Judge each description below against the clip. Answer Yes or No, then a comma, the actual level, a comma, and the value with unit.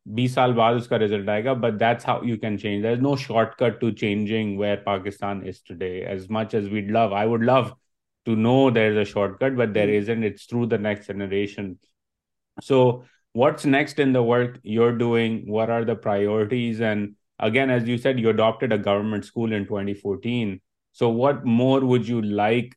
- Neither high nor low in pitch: No, low, 115 Hz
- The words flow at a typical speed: Yes, average, 175 wpm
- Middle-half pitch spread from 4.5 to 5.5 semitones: No, average, 2.8 semitones